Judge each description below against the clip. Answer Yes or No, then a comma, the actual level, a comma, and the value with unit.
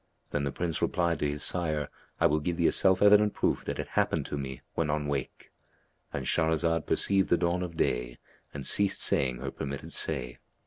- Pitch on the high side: No, very low, 80 Hz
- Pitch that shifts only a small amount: No, average, 3.8 semitones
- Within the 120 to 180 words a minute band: No, average, 195 wpm